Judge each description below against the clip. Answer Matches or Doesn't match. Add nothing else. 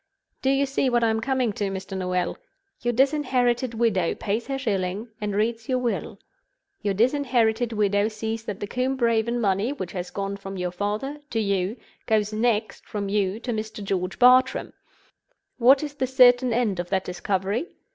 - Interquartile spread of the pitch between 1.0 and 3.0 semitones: Doesn't match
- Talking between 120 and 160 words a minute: Doesn't match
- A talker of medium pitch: Doesn't match